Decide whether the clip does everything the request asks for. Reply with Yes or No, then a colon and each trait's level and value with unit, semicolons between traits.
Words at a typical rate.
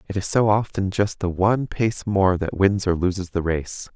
No: fast, 225 wpm